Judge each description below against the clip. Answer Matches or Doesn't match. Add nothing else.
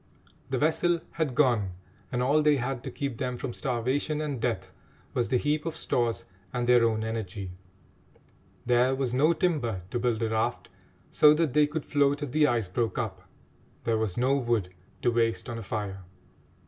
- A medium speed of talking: Matches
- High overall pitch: Doesn't match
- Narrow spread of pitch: Doesn't match